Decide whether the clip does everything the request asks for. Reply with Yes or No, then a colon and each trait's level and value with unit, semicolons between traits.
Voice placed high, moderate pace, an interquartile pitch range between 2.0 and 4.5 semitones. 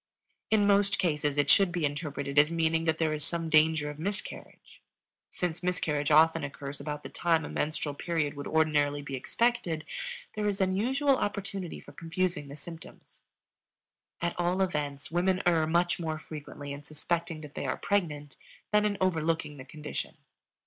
No: medium, 160 Hz; average, 165 wpm; average, 3.5 semitones